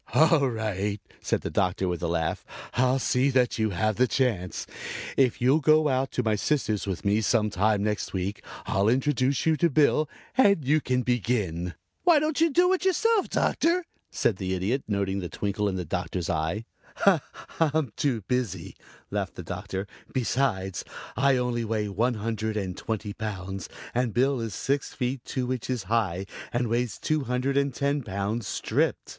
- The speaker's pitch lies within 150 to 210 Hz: No, low, 115 Hz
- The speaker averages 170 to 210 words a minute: Yes, average, 175 wpm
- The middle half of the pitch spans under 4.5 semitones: No, average, 5.2 semitones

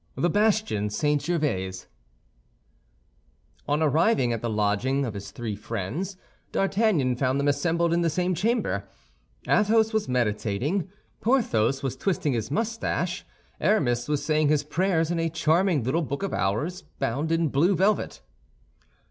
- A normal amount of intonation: No, wide, 6.8 semitones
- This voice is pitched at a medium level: Yes, medium, 150 Hz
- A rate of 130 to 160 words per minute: Yes, average, 140 wpm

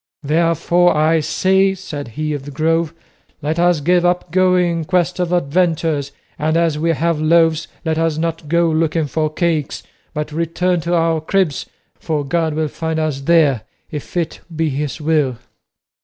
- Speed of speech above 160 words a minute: Yes, average, 170 wpm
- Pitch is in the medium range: Yes, medium, 160 Hz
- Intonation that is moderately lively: No, narrow, 2.0 semitones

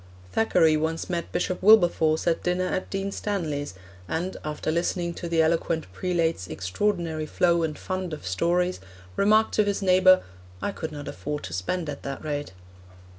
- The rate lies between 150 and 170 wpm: Yes, average, 165 wpm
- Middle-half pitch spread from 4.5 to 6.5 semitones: No, average, 3.0 semitones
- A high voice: No, medium, 170 Hz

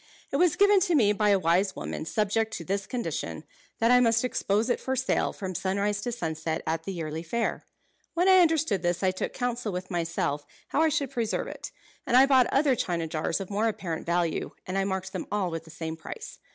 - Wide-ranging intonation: Yes, wide, 6.1 semitones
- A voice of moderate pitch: No, high, 200 Hz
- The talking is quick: Yes, fast, 220 wpm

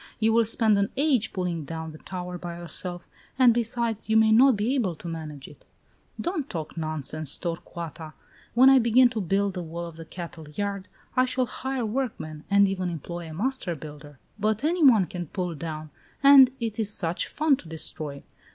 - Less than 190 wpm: No, average, 195 wpm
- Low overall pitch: No, high, 190 Hz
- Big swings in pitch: Yes, wide, 6.2 semitones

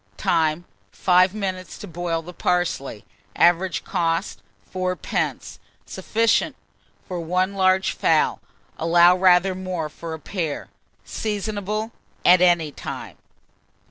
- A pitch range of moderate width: No, narrow, 2.0 semitones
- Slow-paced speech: Yes, slow, 110 wpm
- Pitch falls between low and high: Yes, medium, 180 Hz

